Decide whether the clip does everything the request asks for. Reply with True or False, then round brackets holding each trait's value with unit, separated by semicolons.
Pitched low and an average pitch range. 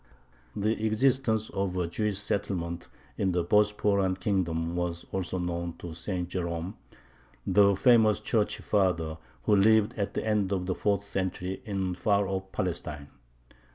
True (95 Hz; 3.0 semitones)